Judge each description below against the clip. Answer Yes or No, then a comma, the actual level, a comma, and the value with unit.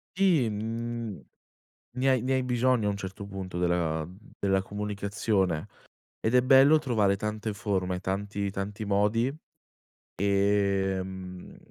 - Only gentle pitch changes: No, average, 3.3 semitones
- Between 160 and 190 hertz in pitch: No, low, 100 Hz